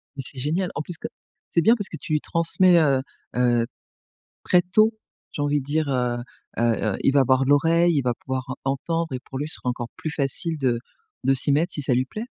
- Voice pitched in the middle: Yes, medium, 145 Hz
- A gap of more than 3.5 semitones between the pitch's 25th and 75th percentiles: Yes, average, 4.2 semitones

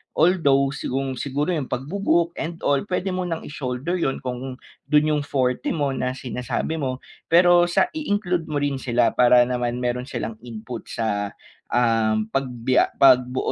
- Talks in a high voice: No, low, 135 Hz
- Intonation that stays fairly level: No, average, 4.5 semitones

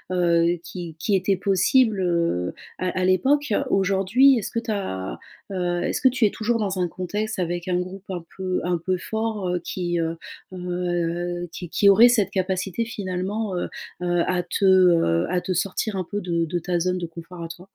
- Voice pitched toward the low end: No, medium, 185 Hz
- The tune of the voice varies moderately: No, narrow, 2.2 semitones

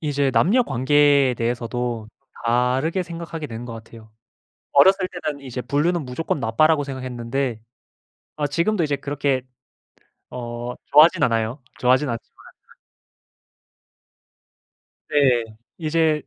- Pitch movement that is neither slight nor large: Yes, average, 4.2 semitones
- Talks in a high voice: No, low, 135 Hz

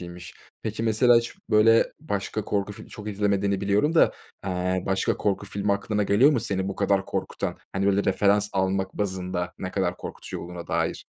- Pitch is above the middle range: No, low, 100 Hz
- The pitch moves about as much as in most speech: No, narrow, 1.8 semitones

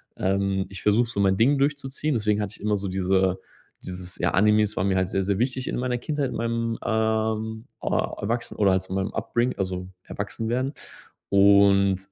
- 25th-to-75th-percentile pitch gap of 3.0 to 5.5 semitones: Yes, average, 3.3 semitones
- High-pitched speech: No, low, 105 Hz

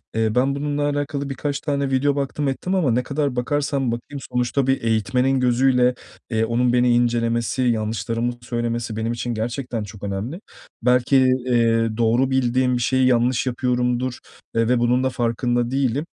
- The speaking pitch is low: Yes, low, 125 Hz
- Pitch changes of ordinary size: No, narrow, 2.3 semitones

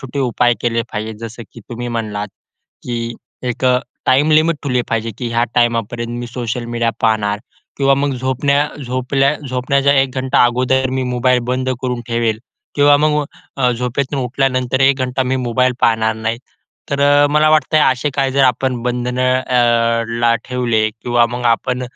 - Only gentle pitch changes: Yes, narrow, 2.1 semitones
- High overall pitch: No, low, 125 Hz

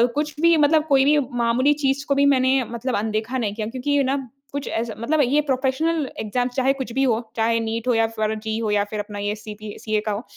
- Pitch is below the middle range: No, high, 245 Hz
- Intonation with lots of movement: No, average, 4.0 semitones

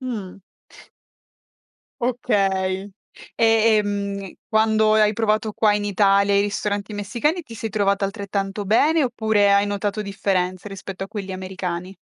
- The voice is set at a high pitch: Yes, high, 205 Hz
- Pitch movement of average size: No, narrow, 1.7 semitones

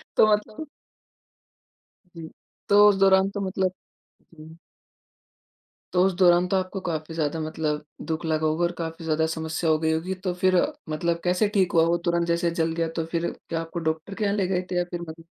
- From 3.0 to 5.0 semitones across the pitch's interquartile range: No, narrow, 2.5 semitones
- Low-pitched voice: No, medium, 170 Hz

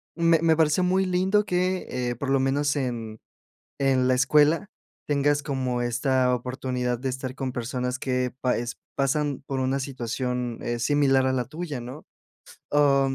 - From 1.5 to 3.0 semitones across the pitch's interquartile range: Yes, average, 2.7 semitones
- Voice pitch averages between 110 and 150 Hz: Yes, low, 135 Hz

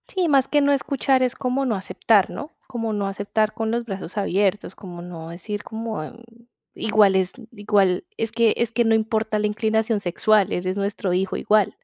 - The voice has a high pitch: Yes, high, 215 Hz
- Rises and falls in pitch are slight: No, average, 3.0 semitones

